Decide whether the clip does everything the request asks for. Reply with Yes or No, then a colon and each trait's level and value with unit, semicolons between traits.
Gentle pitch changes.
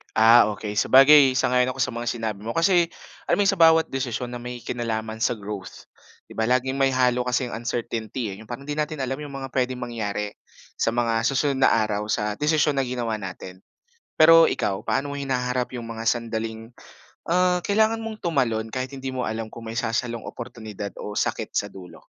No: average, 3.3 semitones